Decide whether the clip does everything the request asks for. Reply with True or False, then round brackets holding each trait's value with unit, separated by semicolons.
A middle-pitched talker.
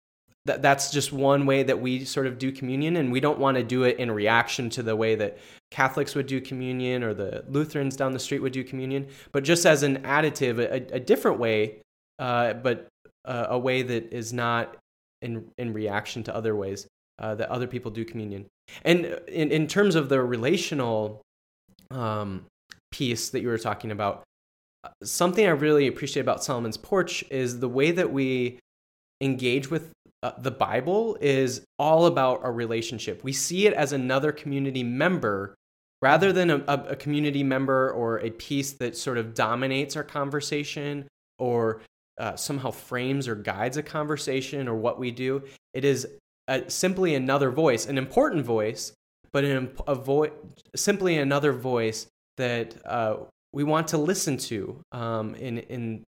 False (130 Hz)